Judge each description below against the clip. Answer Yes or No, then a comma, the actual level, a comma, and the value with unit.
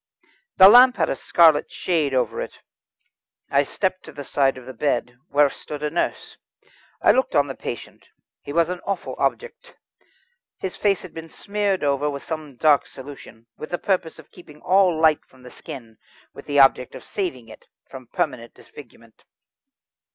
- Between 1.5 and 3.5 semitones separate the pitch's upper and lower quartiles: No, average, 5.2 semitones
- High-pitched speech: No, medium, 150 Hz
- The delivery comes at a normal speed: Yes, average, 175 wpm